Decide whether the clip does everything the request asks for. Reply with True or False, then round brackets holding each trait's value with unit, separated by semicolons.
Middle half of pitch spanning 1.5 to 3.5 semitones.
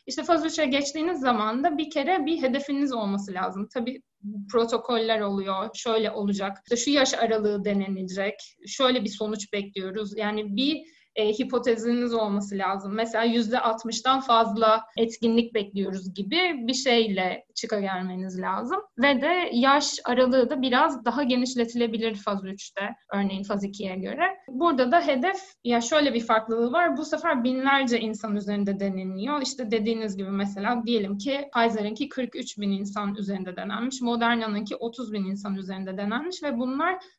False (4.5 semitones)